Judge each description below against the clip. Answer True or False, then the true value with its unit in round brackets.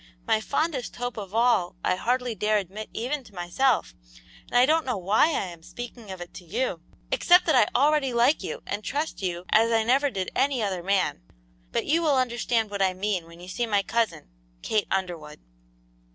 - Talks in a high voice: True (220 Hz)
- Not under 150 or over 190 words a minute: False (200 wpm)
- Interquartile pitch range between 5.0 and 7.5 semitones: True (5.4 semitones)